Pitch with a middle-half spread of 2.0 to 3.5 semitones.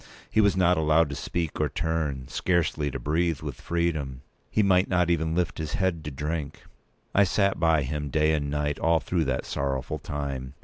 Yes: average, 3.0 semitones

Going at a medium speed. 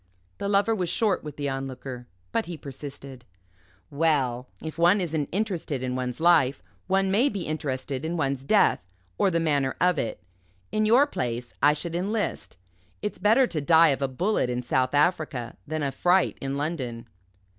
Yes: average, 175 wpm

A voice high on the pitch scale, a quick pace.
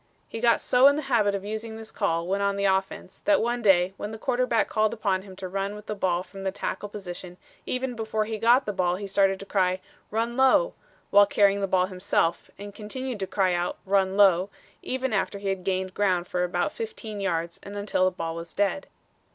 Yes: high, 200 Hz; fast, 225 wpm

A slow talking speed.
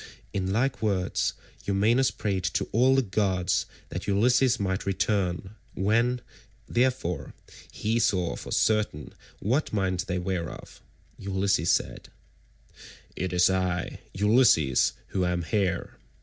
Yes: slow, 120 wpm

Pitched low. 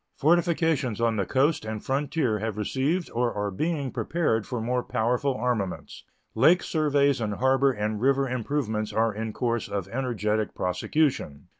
Yes: low, 125 Hz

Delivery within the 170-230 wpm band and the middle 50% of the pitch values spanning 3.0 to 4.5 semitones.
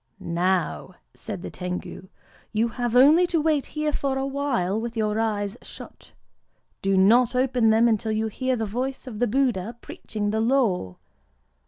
No: average, 160 wpm; average, 4.1 semitones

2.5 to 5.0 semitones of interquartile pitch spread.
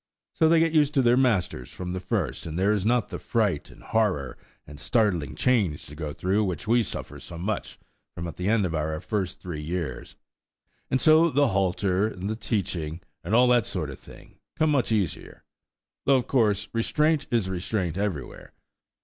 No: wide, 5.6 semitones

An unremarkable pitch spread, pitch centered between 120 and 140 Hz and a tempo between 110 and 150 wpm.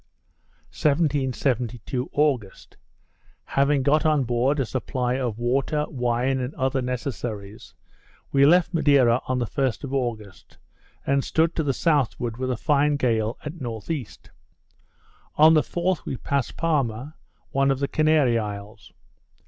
Yes: average, 3.4 semitones; low, 135 Hz; slow, 135 wpm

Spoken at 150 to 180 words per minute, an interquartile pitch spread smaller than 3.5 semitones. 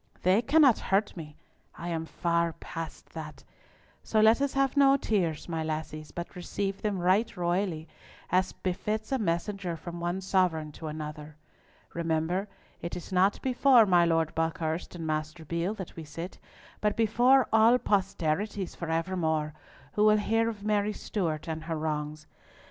No: average, 160 wpm; average, 4.7 semitones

